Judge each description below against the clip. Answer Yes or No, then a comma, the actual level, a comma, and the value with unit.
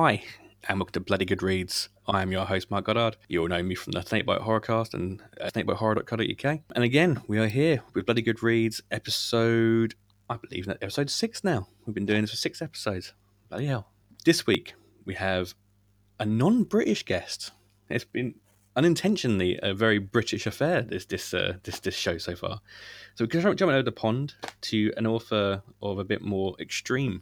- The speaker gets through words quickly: No, average, 190 wpm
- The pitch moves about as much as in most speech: Yes, average, 3.5 semitones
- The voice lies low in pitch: Yes, low, 110 Hz